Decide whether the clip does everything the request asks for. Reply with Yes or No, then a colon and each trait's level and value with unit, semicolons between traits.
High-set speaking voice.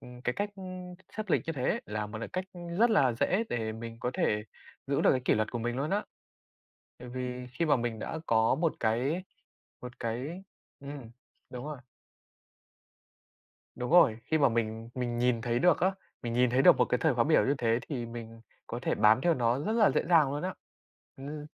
No: low, 125 Hz